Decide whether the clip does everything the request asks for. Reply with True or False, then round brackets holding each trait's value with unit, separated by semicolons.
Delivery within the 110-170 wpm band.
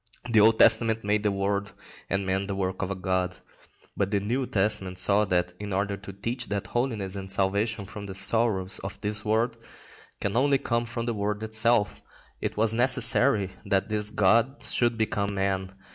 False (185 wpm)